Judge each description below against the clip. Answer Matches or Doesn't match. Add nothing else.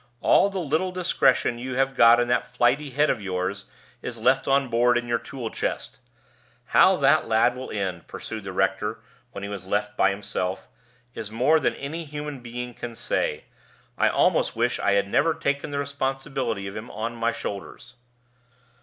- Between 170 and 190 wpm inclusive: Matches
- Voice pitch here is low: Matches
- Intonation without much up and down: Doesn't match